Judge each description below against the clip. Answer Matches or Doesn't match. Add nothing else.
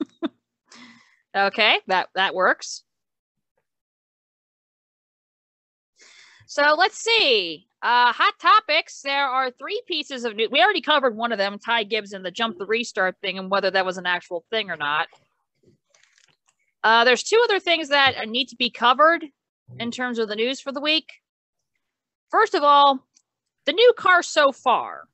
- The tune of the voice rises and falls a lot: Matches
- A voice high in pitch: Matches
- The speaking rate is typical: Matches